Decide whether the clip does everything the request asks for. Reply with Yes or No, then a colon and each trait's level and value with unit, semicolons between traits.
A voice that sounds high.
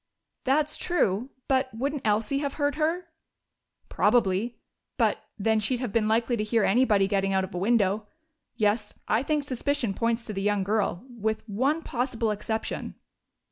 Yes: high, 225 Hz